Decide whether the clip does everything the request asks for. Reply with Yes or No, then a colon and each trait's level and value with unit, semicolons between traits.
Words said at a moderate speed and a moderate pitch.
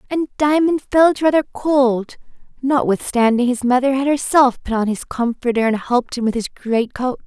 No: average, 165 wpm; very high, 255 Hz